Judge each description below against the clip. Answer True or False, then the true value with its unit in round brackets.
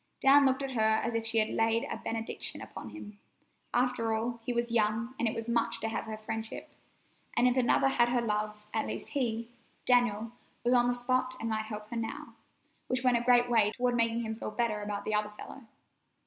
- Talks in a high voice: True (230 Hz)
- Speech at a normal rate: False (220 wpm)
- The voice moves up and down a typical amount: False (1.9 semitones)